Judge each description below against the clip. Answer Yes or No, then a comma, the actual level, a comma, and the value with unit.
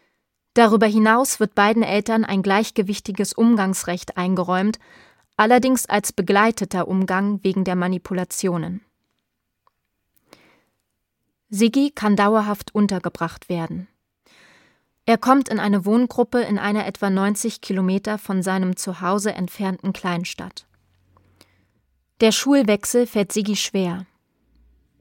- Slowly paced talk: Yes, slow, 100 wpm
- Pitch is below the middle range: No, high, 200 Hz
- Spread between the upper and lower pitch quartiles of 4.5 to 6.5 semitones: No, average, 3.0 semitones